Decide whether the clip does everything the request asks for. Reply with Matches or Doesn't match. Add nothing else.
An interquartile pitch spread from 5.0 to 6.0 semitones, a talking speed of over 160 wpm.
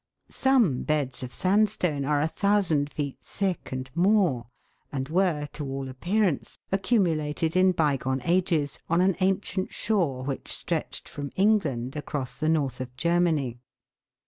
Doesn't match